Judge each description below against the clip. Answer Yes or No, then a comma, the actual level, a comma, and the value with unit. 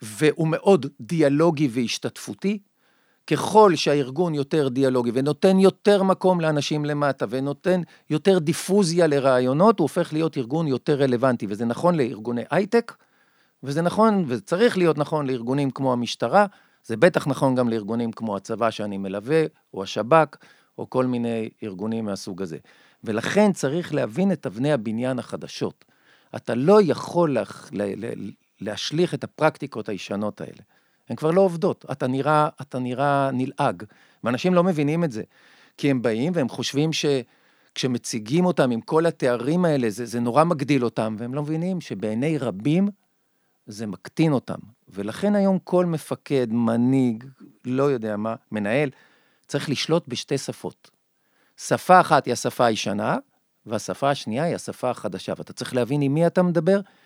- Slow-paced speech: No, average, 145 wpm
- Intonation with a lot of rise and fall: Yes, wide, 6.0 semitones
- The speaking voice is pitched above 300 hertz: No, medium, 145 Hz